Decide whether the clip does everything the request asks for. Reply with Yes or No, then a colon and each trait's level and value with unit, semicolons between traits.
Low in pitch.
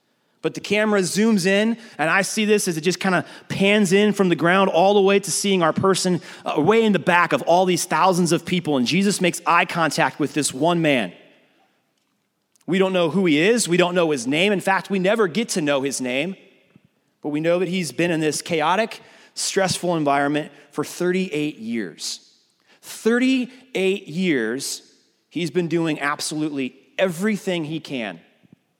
No: medium, 180 Hz